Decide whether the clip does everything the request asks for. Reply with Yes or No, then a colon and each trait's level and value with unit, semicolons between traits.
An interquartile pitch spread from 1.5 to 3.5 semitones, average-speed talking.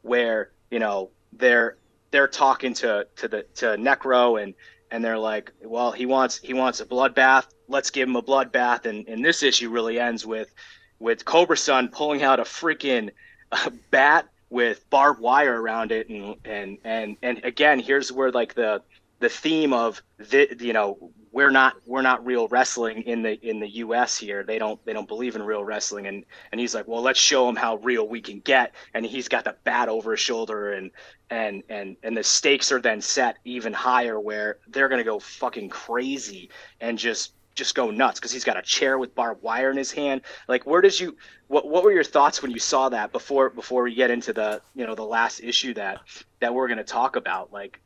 No: average, 3.0 semitones; fast, 210 wpm